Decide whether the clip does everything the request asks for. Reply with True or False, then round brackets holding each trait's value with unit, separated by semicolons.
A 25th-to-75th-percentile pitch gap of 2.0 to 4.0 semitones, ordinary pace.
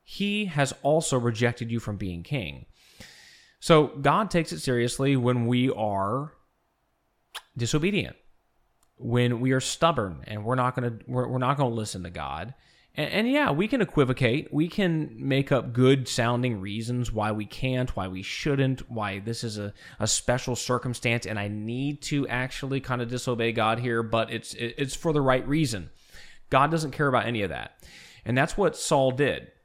True (3.6 semitones; 180 wpm)